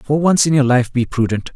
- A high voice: No, low, 135 Hz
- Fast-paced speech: Yes, fast, 270 wpm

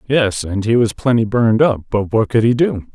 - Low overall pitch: Yes, low, 115 Hz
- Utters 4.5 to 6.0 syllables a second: Yes, 5.3 syllables/s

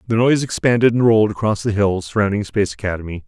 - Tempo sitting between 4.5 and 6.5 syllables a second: No, 7.0 syllables/s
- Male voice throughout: Yes, male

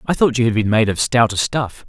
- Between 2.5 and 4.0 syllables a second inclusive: No, 5.7 syllables/s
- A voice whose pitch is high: No, low, 115 Hz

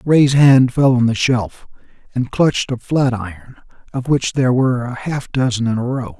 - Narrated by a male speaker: Yes, male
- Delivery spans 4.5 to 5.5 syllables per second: Yes, 5.0 syllables/s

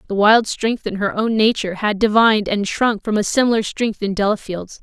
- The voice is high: Yes, high, 210 Hz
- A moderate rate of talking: No, fast, 210 wpm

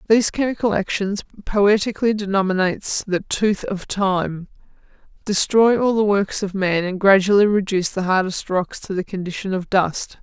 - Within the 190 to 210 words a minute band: No, average, 155 wpm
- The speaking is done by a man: No, female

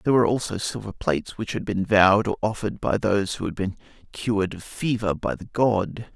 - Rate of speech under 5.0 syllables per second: No, 5.9 syllables/s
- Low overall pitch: Yes, low, 105 Hz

